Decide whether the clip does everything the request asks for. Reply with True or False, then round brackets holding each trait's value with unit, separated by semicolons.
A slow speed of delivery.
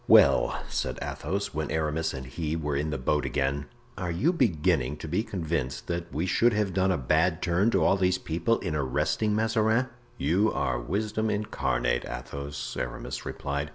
False (175 wpm)